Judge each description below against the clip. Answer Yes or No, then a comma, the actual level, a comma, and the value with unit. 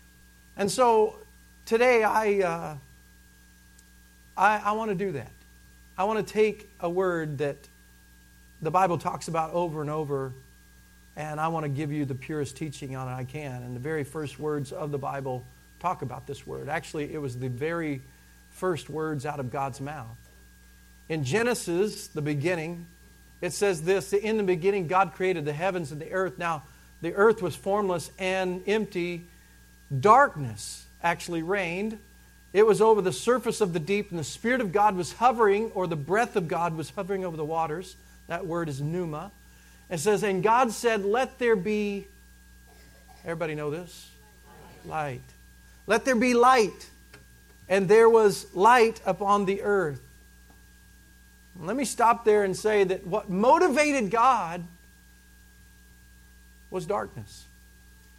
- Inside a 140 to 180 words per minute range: Yes, average, 160 wpm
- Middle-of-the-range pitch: Yes, medium, 160 Hz